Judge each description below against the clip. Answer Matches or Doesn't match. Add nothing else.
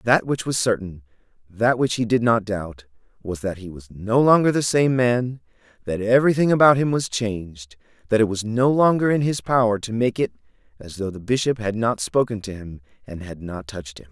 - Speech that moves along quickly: Matches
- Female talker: Doesn't match